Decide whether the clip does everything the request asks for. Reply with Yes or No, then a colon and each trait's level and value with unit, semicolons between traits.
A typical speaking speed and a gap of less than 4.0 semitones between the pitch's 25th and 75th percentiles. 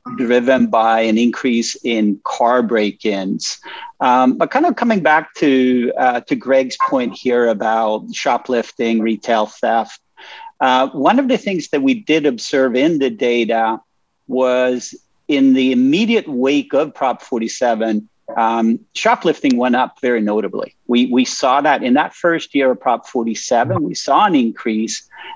No: average, 155 wpm; average, 4.9 semitones